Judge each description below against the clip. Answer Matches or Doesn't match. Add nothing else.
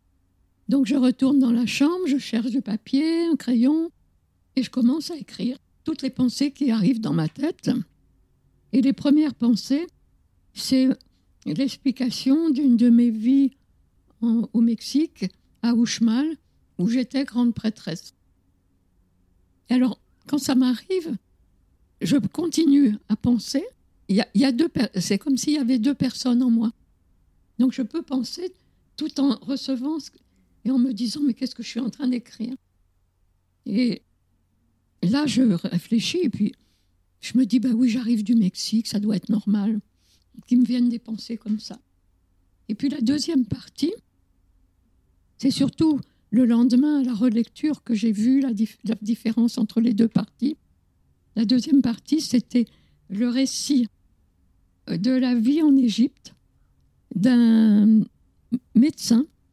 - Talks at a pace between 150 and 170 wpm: Matches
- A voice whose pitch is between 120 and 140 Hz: Doesn't match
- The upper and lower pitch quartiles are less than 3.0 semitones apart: Doesn't match